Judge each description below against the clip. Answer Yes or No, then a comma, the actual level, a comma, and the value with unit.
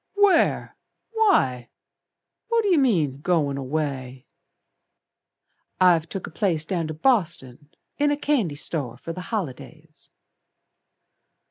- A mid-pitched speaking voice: Yes, medium, 165 Hz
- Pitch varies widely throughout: Yes, wide, 8.6 semitones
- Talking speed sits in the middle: No, slow, 110 wpm